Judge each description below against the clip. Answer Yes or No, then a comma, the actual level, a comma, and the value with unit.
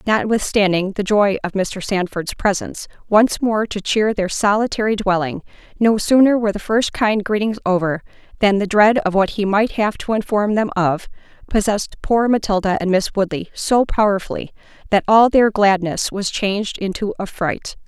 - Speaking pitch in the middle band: No, high, 205 Hz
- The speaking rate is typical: Yes, average, 170 wpm